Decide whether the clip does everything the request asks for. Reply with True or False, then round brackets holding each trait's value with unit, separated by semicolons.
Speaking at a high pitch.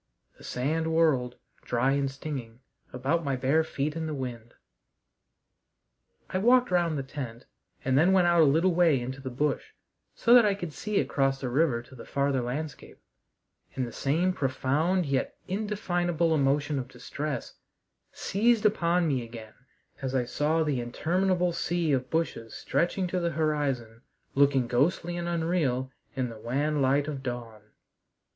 False (145 Hz)